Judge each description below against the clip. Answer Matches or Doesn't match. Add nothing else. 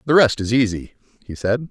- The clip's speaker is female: Doesn't match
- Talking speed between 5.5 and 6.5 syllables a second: Matches